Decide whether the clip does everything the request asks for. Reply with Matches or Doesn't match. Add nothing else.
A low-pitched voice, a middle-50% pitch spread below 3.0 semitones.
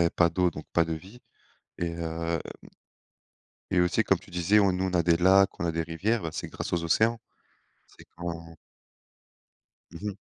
Matches